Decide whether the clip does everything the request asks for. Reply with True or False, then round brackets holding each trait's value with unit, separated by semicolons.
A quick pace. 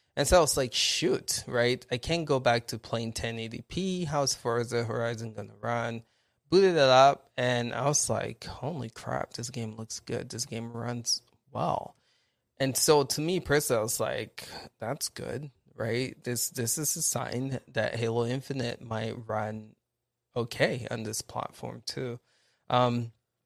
False (170 wpm)